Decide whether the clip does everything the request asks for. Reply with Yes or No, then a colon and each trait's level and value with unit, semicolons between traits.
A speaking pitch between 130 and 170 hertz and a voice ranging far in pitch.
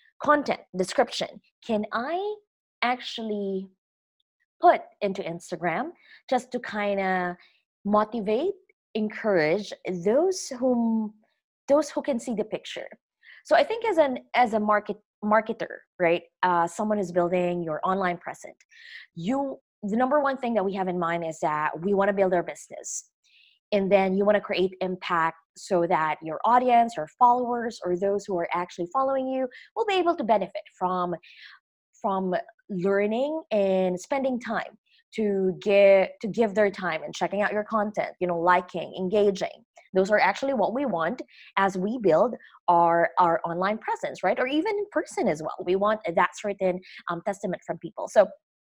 No: high, 205 Hz; wide, 5.9 semitones